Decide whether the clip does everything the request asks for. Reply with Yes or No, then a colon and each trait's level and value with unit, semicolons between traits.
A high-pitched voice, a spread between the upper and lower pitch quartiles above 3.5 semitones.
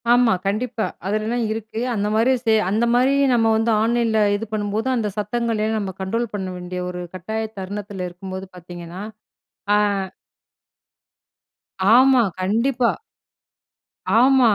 No: high, 220 Hz; average, 3.2 semitones